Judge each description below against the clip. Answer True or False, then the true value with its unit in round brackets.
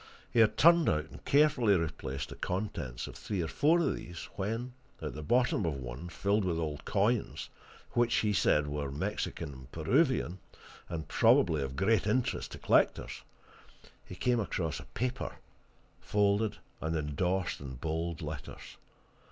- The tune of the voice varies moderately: False (6.3 semitones)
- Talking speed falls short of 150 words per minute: False (155 wpm)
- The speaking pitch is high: False (90 Hz)